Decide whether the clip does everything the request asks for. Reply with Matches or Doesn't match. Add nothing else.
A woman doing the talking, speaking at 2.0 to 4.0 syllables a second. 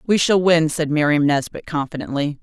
Doesn't match